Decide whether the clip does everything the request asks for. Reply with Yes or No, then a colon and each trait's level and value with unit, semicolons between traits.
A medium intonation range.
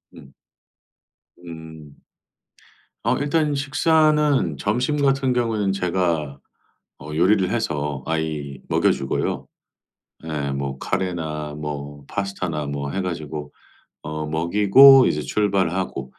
No: wide, 6.3 semitones